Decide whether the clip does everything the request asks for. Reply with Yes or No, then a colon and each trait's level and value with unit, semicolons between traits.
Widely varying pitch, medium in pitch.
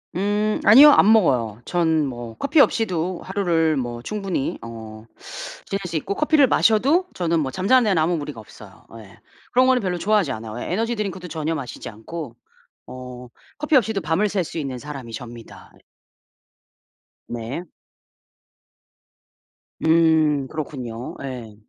Yes: wide, 8.3 semitones; medium, 160 Hz